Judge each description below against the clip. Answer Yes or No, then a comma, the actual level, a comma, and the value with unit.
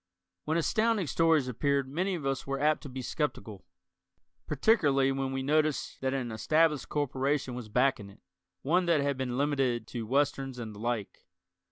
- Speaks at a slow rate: No, average, 170 wpm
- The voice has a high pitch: No, low, 135 Hz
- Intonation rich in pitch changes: No, average, 3.1 semitones